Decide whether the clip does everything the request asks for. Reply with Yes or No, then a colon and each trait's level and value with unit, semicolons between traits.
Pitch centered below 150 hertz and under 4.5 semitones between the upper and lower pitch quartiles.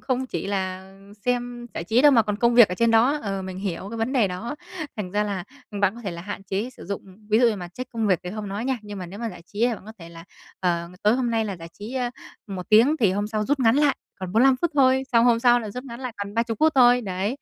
No: high, 220 Hz; average, 4.0 semitones